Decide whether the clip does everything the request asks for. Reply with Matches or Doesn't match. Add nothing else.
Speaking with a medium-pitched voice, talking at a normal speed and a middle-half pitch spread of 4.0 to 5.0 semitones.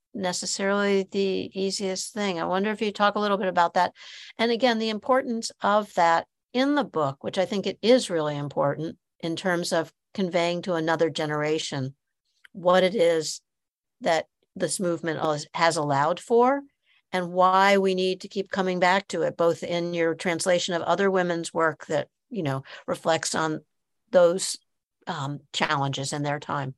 Doesn't match